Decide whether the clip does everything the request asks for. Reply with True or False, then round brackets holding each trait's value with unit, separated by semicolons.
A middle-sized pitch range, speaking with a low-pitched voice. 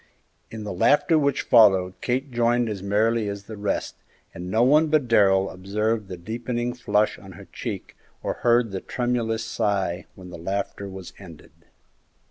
True (3.8 semitones; 105 Hz)